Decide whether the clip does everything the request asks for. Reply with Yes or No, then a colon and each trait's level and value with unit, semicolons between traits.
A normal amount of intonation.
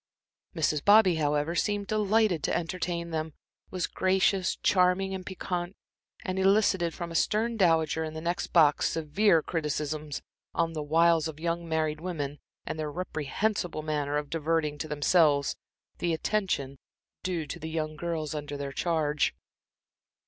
Yes: average, 3.2 semitones